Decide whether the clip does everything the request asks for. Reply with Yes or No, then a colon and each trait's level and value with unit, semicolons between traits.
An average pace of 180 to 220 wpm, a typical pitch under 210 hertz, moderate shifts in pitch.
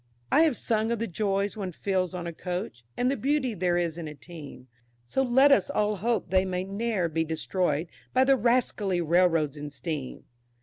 No: average, 200 wpm; medium, 185 Hz; wide, 5.7 semitones